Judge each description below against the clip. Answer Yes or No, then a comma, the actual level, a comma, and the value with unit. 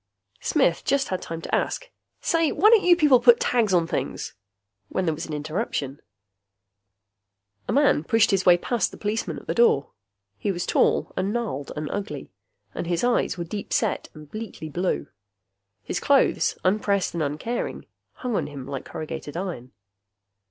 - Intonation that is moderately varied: No, wide, 7.2 semitones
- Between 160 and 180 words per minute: Yes, average, 170 wpm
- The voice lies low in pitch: No, high, 190 Hz